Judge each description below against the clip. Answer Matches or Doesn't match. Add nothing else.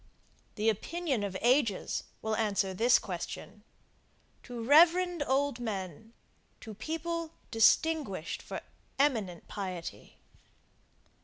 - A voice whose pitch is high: Matches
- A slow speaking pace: Matches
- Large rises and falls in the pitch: Matches